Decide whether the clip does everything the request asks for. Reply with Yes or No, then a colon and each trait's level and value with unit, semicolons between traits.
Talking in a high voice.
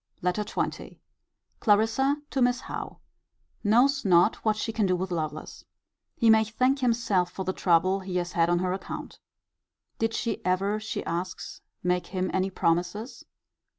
Yes: high, 195 Hz